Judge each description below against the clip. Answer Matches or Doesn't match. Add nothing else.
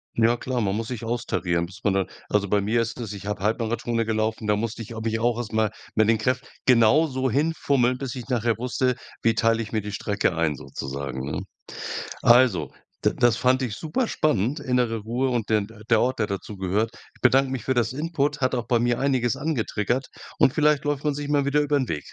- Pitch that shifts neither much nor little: Matches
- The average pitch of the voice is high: Doesn't match